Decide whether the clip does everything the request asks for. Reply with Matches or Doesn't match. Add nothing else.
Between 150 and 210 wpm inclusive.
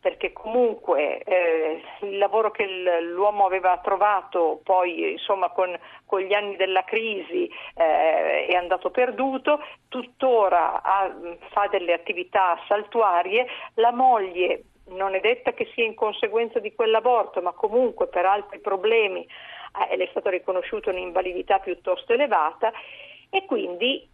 Doesn't match